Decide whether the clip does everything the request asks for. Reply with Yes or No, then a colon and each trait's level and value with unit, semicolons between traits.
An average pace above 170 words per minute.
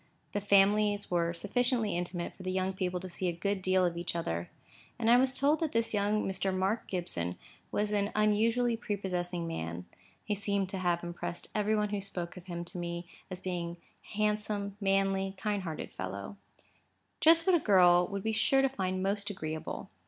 Yes: average, 190 wpm